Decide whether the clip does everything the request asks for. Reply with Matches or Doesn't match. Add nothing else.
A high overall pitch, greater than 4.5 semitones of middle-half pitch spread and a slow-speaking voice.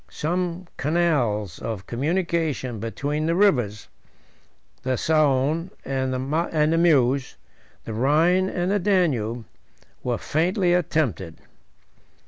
Doesn't match